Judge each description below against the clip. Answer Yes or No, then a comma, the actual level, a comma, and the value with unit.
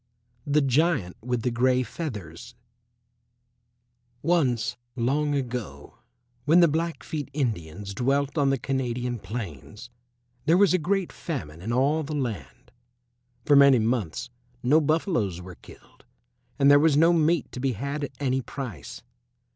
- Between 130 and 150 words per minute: Yes, average, 140 wpm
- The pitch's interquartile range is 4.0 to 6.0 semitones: Yes, average, 4.5 semitones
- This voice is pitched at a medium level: No, low, 130 Hz